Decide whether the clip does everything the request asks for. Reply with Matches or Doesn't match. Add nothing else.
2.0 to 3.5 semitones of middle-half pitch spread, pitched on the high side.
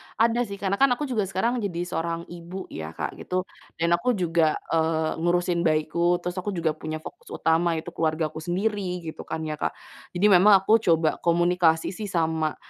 Doesn't match